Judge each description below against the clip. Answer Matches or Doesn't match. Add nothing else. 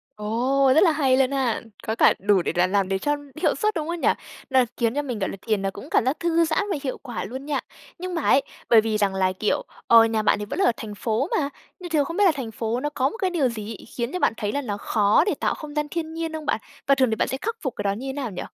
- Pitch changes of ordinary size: Doesn't match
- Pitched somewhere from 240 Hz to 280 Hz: Matches